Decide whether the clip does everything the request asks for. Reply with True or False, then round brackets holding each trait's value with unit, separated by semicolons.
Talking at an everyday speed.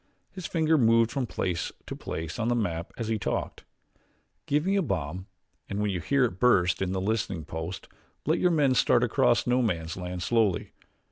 True (195 wpm)